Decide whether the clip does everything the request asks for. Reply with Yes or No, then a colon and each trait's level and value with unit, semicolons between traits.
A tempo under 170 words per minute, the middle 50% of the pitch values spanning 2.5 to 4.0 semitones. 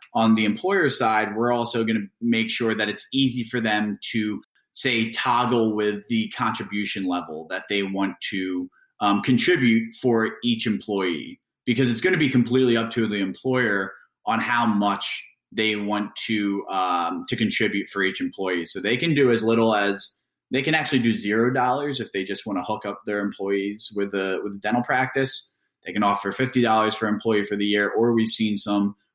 No: average, 195 wpm; average, 2.8 semitones